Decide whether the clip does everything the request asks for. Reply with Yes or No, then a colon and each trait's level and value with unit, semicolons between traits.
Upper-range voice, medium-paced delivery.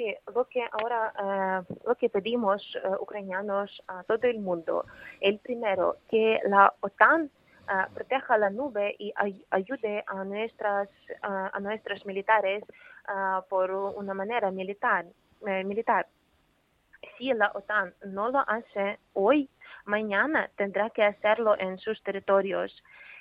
Yes: high, 205 Hz; average, 135 wpm